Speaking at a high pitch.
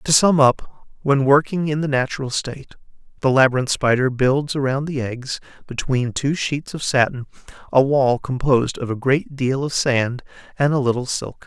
No: low, 135 Hz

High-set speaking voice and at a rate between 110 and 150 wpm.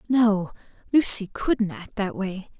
Yes: high, 205 Hz; average, 140 wpm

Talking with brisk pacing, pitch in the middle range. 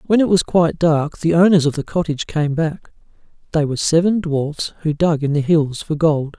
Yes: fast, 215 wpm; medium, 160 Hz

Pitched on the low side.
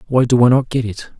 Yes: low, 125 Hz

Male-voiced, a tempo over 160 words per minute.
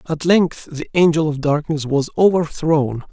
No: male; average, 155 wpm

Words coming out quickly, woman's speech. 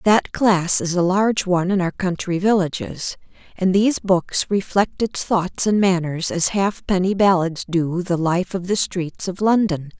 No: average, 180 wpm; female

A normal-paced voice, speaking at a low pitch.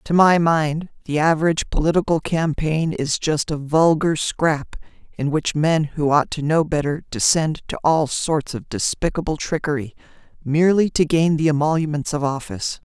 No: average, 160 wpm; medium, 155 Hz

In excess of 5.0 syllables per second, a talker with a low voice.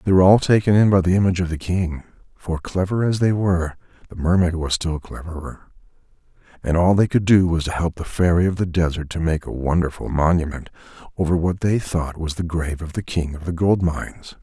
Yes: 5.9 syllables/s; very low, 85 Hz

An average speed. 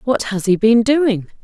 No: fast, 210 wpm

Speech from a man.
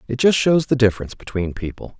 Yes: male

